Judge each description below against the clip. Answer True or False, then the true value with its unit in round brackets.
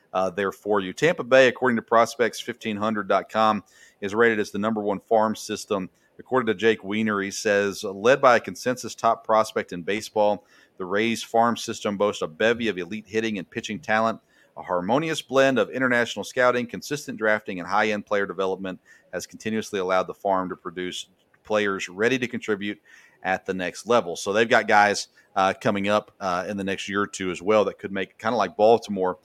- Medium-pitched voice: False (105 Hz)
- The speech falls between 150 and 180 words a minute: False (195 wpm)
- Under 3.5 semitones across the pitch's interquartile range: True (2.5 semitones)